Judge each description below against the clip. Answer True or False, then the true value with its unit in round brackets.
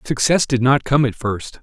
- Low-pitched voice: True (130 Hz)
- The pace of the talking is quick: True (220 wpm)